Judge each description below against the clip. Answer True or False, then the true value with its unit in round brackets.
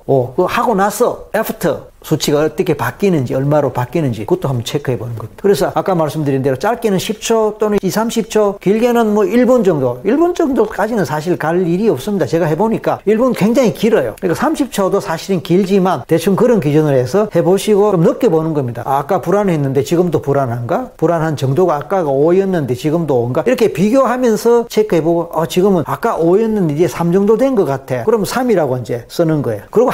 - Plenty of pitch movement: True (5.9 semitones)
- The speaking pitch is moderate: True (180 Hz)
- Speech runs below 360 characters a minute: False (405 characters per minute)